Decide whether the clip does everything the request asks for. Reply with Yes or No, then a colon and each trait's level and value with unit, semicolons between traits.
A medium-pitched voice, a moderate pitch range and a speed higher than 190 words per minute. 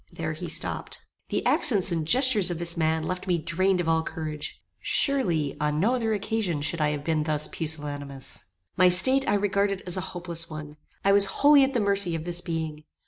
Yes: medium, 175 Hz; average, 4.2 semitones; average, 200 wpm